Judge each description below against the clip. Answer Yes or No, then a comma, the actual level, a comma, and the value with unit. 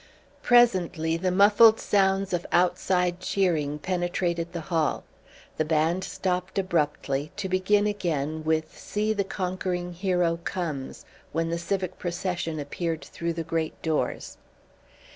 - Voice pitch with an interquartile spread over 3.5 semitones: No, narrow, 2.6 semitones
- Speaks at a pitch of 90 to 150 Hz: No, medium, 175 Hz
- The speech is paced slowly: Yes, slow, 125 wpm